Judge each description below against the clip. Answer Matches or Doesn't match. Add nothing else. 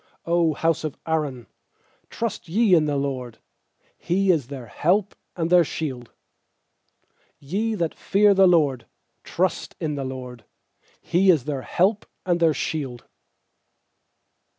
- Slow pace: Matches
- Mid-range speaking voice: Matches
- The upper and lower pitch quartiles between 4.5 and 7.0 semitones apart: Matches